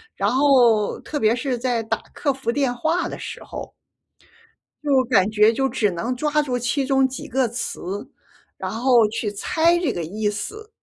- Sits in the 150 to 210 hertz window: No, very high, 250 Hz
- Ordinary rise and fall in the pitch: Yes, average, 4.0 semitones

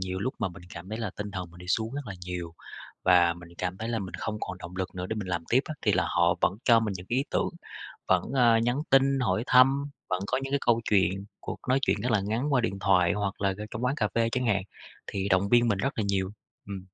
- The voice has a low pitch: Yes, low, 105 Hz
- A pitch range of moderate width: Yes, average, 4.3 semitones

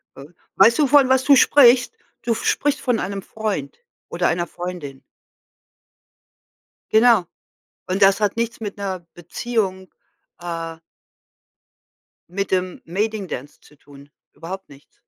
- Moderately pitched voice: No, high, 195 Hz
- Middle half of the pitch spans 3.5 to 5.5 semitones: Yes, average, 5.1 semitones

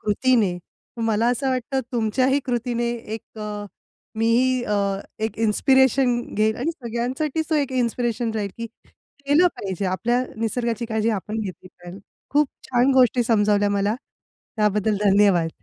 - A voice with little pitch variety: No, average, 3.3 semitones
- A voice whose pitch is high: Yes, high, 230 Hz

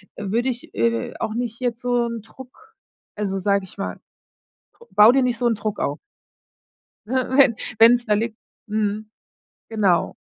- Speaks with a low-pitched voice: No, high, 225 Hz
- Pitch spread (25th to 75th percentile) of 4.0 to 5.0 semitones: No, average, 2.8 semitones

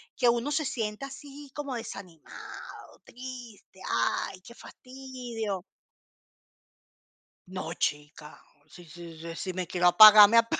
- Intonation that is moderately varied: No, wide, 6.4 semitones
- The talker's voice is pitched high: Yes, high, 215 Hz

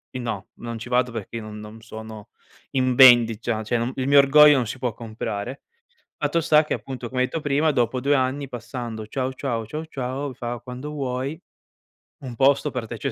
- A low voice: Yes, low, 125 Hz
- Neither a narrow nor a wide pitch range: Yes, average, 3.1 semitones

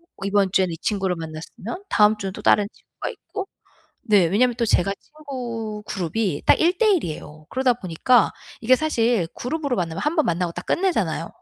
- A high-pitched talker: Yes, high, 215 Hz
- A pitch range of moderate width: No, wide, 6.1 semitones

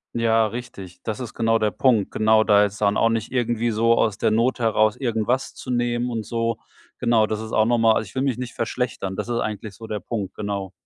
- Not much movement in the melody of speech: Yes, narrow, 1.9 semitones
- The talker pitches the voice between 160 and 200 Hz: No, low, 115 Hz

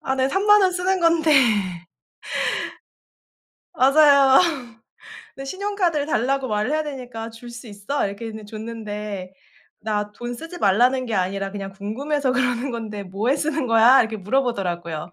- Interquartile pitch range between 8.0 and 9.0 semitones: No, average, 5.3 semitones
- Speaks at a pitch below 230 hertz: No, high, 240 Hz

